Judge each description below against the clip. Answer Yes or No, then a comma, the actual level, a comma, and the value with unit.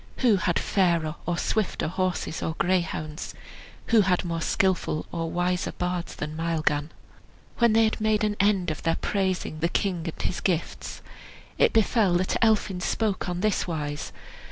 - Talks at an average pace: Yes, average, 165 wpm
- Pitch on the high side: No, medium, 180 Hz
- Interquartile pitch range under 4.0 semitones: Yes, average, 3.4 semitones